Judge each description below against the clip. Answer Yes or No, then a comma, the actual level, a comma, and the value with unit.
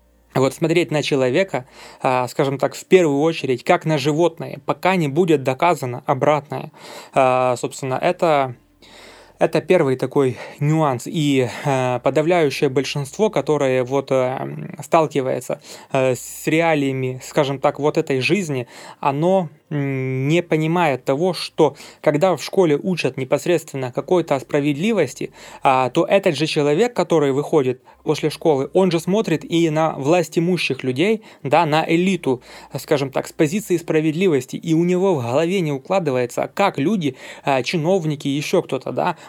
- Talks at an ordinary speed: Yes, average, 140 wpm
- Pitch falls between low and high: Yes, medium, 150 Hz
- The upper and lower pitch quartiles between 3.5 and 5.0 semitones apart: Yes, average, 4.1 semitones